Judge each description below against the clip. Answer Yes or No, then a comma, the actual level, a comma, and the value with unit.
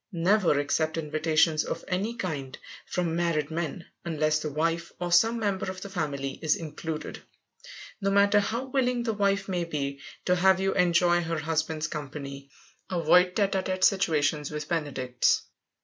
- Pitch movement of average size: Yes, average, 3.8 semitones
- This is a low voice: No, medium, 170 Hz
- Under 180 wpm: Yes, average, 160 wpm